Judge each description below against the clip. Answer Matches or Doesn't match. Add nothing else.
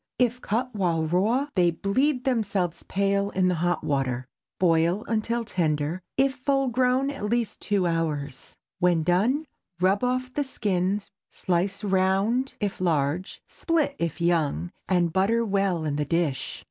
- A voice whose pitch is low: Doesn't match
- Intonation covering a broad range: Matches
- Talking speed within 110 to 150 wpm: Matches